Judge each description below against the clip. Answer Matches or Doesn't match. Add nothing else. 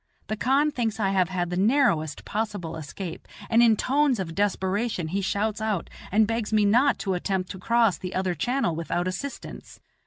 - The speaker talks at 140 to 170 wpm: Doesn't match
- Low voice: Doesn't match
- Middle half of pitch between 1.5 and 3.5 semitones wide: Doesn't match